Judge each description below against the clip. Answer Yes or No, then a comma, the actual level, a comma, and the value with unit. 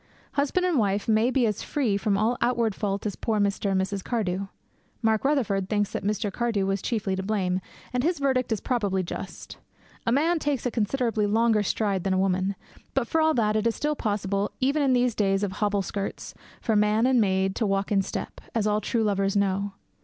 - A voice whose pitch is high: Yes, high, 210 Hz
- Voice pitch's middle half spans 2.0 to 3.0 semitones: No, average, 3.4 semitones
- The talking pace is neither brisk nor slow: No, fast, 215 wpm